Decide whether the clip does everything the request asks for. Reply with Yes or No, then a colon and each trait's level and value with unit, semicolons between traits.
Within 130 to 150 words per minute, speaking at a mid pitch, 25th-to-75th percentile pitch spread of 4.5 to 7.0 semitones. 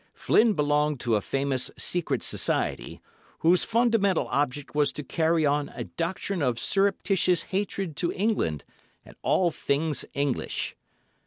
Yes: slow, 135 wpm; medium, 160 Hz; average, 5.1 semitones